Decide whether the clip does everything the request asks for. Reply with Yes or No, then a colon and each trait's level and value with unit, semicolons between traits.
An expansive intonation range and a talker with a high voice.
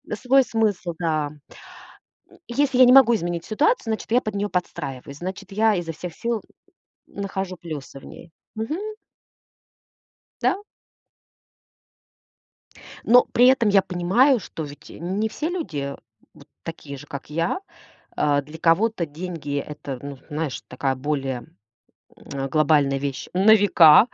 No: wide, 7.1 semitones; medium, 175 Hz